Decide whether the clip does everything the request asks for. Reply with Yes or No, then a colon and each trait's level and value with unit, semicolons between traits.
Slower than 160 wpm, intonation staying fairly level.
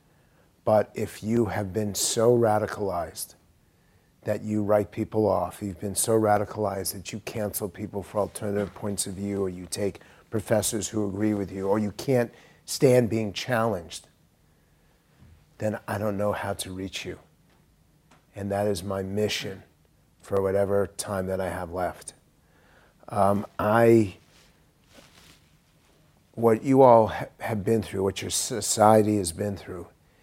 Yes: average, 145 wpm; narrow, 1.8 semitones